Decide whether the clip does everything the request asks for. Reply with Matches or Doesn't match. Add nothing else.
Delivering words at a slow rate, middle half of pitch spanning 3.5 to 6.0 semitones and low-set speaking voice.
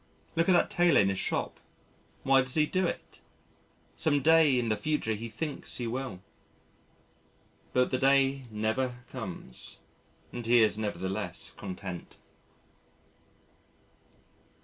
Matches